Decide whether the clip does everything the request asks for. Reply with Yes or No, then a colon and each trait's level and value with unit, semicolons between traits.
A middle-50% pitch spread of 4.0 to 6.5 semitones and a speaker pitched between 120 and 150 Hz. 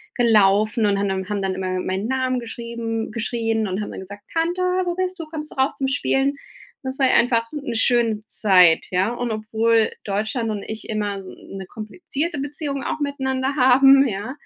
No: average, 4.5 semitones; high, 230 Hz